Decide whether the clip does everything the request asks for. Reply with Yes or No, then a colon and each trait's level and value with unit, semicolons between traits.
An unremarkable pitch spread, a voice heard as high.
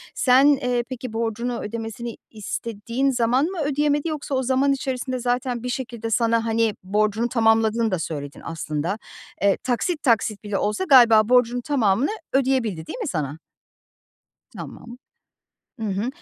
Yes: average, 3.2 semitones; high, 235 Hz